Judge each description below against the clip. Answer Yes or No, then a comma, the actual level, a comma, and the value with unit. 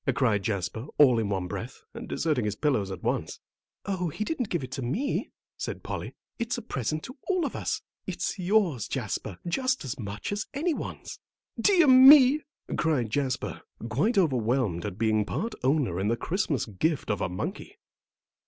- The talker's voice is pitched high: No, medium, 140 Hz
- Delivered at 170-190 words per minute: Yes, average, 175 wpm